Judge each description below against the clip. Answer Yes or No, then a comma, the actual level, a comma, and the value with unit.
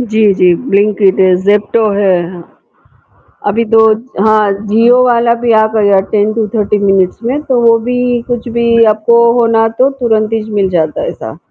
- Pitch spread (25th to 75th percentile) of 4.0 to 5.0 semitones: No, narrow, 2.4 semitones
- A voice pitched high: Yes, high, 220 Hz